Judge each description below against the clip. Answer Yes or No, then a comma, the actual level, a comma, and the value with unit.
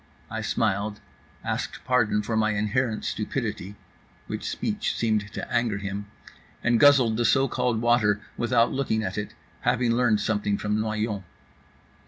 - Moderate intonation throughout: No, narrow, 2.3 semitones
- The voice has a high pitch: No, low, 110 Hz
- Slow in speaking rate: No, average, 145 wpm